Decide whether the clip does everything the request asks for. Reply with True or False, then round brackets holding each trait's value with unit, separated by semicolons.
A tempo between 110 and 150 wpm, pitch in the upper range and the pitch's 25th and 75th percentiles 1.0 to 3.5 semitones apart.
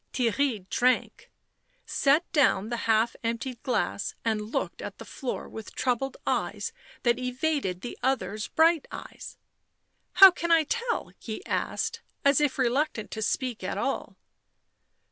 False (145 wpm; 255 Hz; 4.8 semitones)